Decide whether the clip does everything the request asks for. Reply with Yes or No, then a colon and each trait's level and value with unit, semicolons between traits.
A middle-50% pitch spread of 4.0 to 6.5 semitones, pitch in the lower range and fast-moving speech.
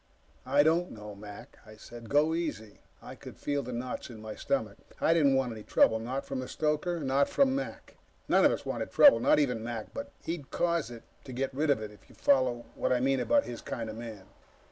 Yes: average, 5.0 semitones; low, 130 Hz; fast, 230 wpm